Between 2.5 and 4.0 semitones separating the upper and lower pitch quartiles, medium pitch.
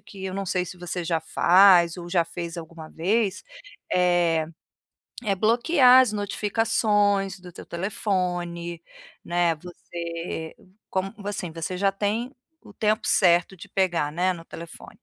Yes: average, 2.9 semitones; medium, 180 Hz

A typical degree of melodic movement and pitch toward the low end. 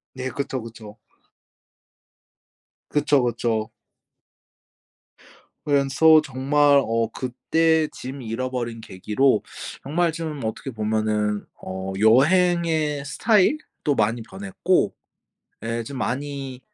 Yes: average, 4.9 semitones; low, 130 Hz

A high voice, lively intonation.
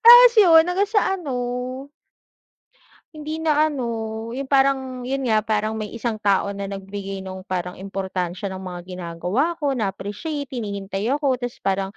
Yes: high, 225 Hz; wide, 6.1 semitones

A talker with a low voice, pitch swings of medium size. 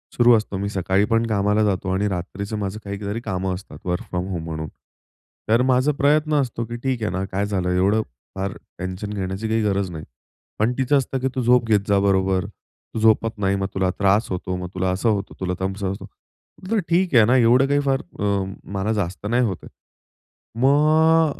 Yes: low, 105 Hz; average, 4.1 semitones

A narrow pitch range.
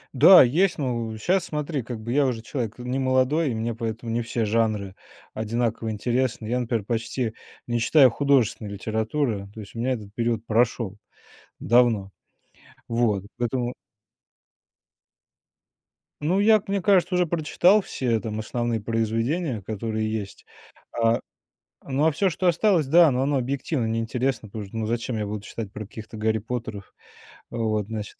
No: average, 3.5 semitones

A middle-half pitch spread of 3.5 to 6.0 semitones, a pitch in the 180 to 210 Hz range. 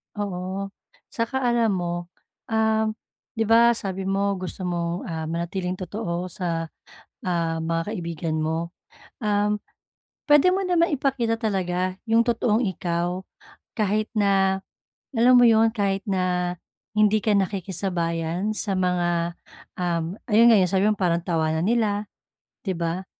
Yes: average, 3.9 semitones; high, 190 Hz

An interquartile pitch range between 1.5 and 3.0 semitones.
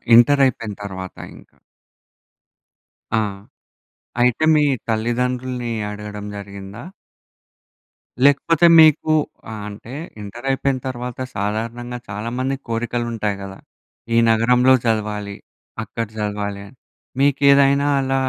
No: average, 3.8 semitones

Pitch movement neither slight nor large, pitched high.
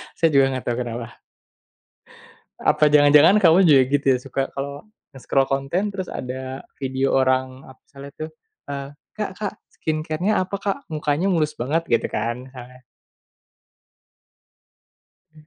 No: average, 3.5 semitones; medium, 140 Hz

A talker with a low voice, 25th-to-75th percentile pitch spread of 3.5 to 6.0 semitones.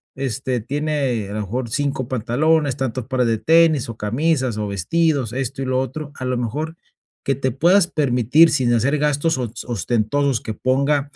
Yes: low, 130 Hz; average, 3.8 semitones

